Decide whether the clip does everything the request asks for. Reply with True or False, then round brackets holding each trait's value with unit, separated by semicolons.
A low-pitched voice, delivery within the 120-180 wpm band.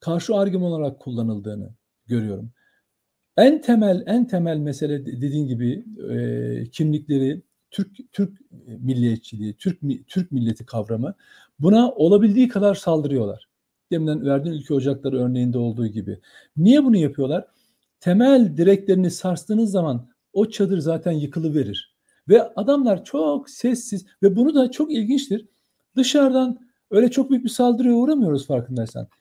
False (170 Hz; 125 wpm)